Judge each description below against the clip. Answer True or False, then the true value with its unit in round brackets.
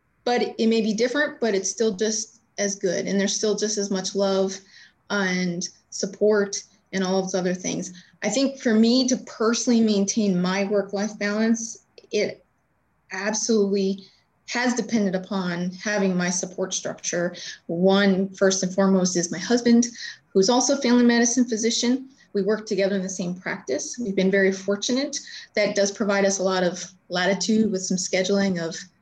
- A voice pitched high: True (200 Hz)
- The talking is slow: False (165 wpm)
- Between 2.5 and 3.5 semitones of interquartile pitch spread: True (2.9 semitones)